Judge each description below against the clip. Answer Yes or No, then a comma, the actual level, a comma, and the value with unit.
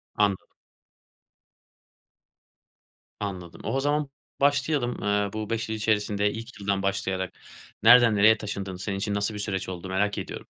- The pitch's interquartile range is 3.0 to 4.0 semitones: No, narrow, 2.4 semitones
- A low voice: Yes, low, 105 Hz